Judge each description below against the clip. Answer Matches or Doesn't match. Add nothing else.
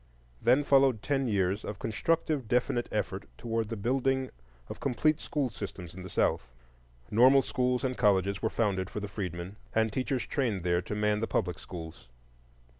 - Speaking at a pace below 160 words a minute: Doesn't match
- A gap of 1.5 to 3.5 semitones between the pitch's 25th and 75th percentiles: Doesn't match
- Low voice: Matches